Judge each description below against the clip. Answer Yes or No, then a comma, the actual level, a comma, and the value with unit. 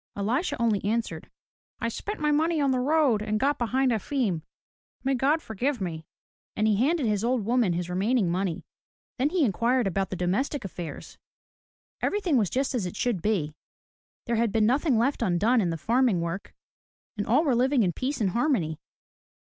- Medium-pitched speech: No, high, 235 Hz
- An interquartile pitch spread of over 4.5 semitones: Yes, wide, 5.5 semitones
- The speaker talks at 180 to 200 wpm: Yes, average, 185 wpm